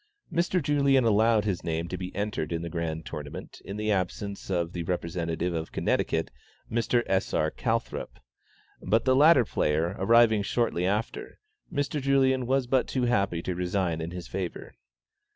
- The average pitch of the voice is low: Yes, low, 100 Hz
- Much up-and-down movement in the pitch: Yes, wide, 6.1 semitones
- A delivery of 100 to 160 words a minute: No, average, 170 wpm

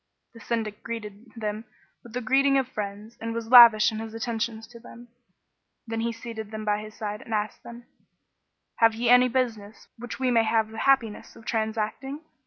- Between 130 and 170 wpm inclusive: No, average, 190 wpm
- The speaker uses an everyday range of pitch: No, narrow, 1.7 semitones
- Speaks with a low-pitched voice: No, high, 225 Hz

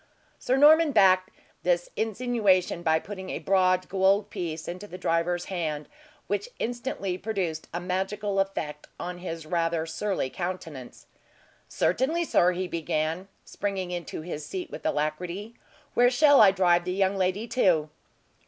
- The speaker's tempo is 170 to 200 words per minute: No, average, 145 wpm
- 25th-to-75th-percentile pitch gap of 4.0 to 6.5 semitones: No, average, 3.0 semitones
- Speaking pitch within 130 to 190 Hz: Yes, medium, 185 Hz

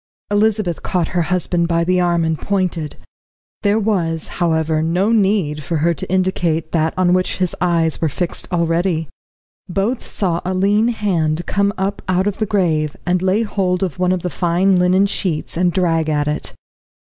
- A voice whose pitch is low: No, medium, 180 Hz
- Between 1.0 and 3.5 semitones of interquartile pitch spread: Yes, average, 2.8 semitones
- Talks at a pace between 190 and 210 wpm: No, average, 180 wpm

